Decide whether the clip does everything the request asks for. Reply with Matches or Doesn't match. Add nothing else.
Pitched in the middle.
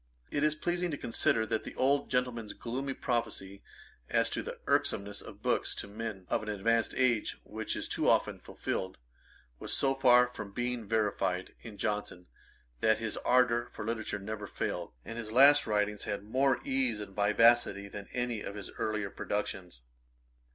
Doesn't match